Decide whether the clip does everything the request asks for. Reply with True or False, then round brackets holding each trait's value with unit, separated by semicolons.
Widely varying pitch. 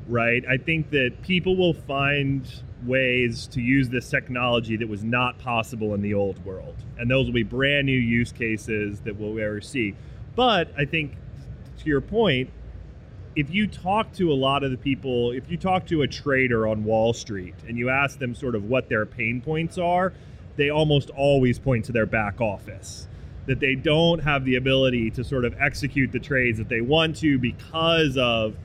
False (3.7 semitones)